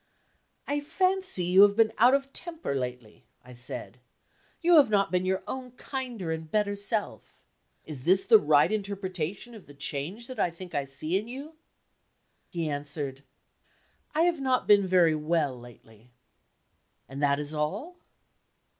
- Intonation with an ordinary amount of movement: No, wide, 8.4 semitones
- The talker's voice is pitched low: No, medium, 185 Hz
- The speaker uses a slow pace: No, average, 155 wpm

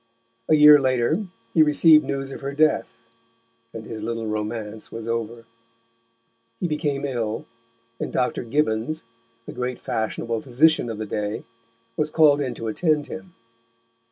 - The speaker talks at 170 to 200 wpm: No, average, 145 wpm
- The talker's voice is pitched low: Yes, low, 125 Hz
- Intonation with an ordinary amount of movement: Yes, average, 5.0 semitones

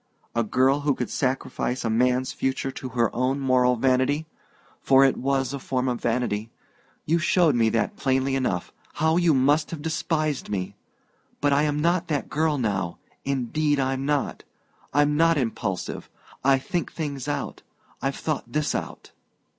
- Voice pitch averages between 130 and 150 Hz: Yes, low, 135 Hz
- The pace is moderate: Yes, average, 160 wpm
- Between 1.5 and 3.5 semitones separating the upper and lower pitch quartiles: Yes, average, 2.9 semitones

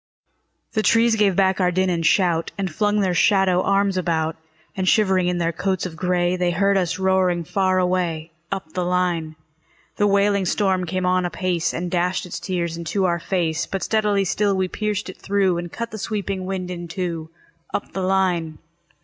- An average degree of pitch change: No, narrow, 2.0 semitones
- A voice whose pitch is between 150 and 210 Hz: Yes, medium, 185 Hz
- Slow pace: No, average, 190 wpm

